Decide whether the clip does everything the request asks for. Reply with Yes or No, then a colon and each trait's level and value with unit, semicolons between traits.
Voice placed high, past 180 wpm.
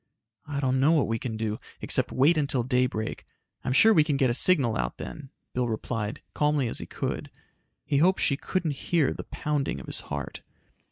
No: low, 135 Hz; average, 200 wpm